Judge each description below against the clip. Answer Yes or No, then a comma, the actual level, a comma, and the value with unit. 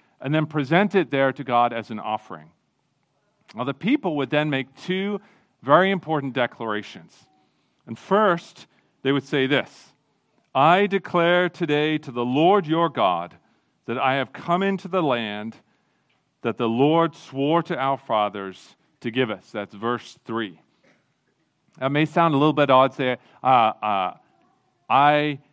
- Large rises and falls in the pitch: Yes, wide, 5.8 semitones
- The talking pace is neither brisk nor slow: Yes, average, 155 wpm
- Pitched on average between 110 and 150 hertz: Yes, medium, 140 Hz